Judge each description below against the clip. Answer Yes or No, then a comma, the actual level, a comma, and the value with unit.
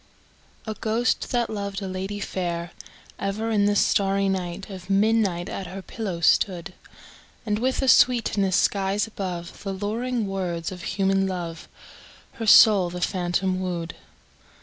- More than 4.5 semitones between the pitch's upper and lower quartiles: No, narrow, 2.5 semitones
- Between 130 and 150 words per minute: Yes, average, 145 wpm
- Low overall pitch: No, high, 195 Hz